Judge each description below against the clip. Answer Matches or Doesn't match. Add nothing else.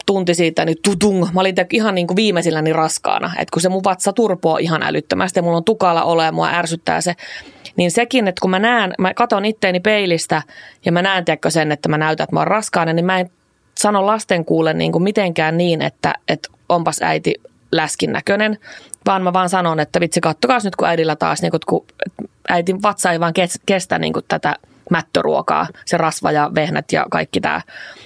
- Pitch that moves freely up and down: Doesn't match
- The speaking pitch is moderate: Matches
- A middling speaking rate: Doesn't match